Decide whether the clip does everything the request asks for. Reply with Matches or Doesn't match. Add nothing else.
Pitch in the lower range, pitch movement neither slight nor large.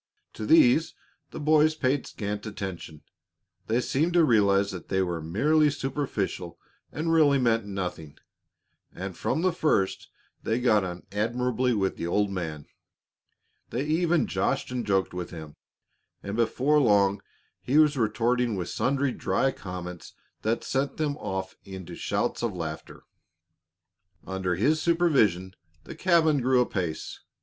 Doesn't match